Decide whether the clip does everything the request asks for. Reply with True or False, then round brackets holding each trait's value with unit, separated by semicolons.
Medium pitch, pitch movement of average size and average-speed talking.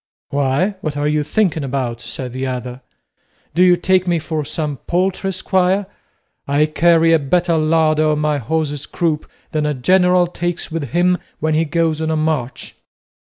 True (155 Hz; 3.2 semitones; 170 wpm)